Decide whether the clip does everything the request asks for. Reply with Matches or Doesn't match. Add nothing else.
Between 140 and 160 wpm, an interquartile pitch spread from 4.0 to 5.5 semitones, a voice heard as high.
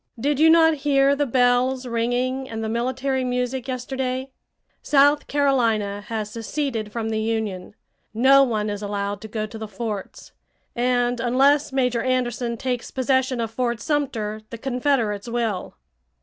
Doesn't match